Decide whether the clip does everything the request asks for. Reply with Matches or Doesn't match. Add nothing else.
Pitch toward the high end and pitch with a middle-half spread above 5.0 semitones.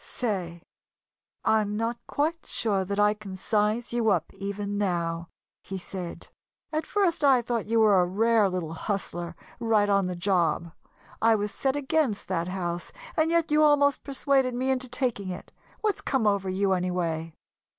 Matches